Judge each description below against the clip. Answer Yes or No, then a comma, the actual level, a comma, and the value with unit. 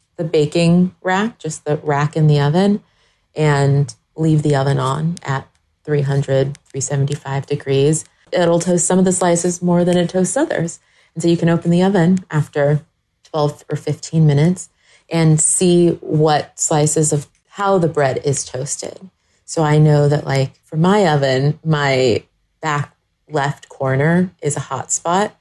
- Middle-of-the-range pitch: Yes, medium, 150 Hz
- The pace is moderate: Yes, average, 160 wpm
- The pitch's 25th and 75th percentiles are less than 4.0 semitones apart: Yes, average, 3.1 semitones